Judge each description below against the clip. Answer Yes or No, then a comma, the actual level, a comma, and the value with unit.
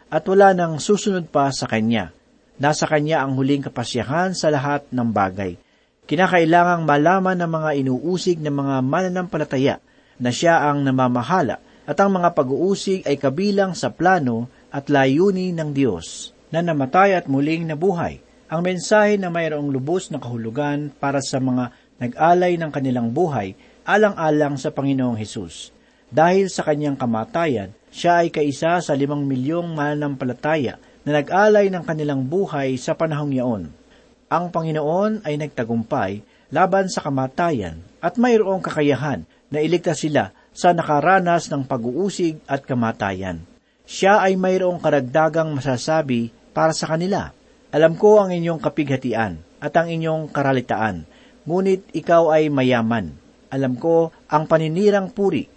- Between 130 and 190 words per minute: Yes, average, 135 wpm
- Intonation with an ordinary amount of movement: Yes, average, 4.7 semitones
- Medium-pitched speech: Yes, medium, 155 Hz